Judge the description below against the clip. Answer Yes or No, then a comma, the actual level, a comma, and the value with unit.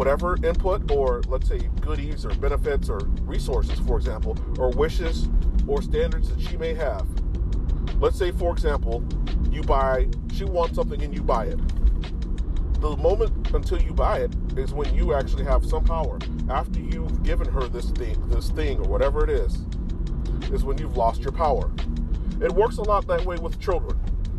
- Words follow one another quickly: No, average, 175 wpm